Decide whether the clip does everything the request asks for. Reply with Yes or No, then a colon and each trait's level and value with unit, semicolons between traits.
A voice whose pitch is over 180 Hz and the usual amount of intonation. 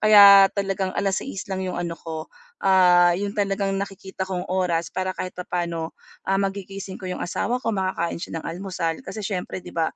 No: high, 190 Hz; narrow, 1.8 semitones